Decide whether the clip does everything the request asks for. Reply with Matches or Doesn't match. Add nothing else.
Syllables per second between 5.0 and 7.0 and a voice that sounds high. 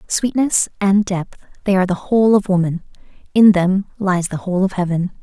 Matches